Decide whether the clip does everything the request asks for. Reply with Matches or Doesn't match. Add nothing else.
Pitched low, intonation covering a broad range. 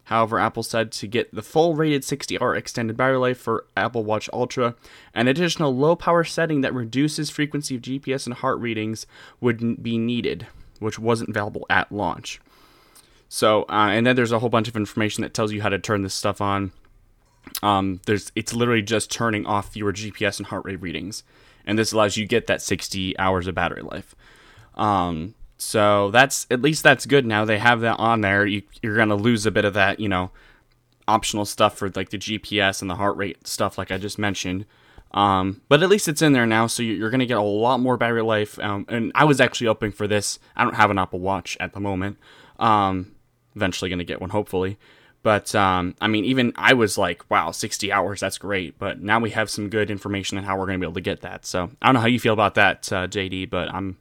Doesn't match